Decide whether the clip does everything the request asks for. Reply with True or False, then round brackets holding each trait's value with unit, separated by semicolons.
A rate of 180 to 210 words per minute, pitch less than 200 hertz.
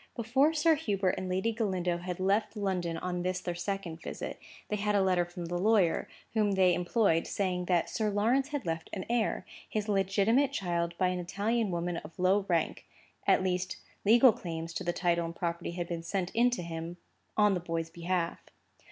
True (190 wpm; 185 Hz)